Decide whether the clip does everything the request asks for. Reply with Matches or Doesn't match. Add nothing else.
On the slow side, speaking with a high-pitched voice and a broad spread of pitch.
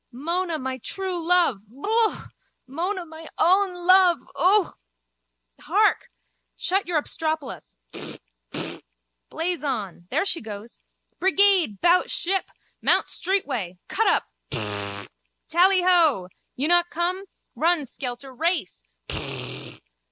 Matches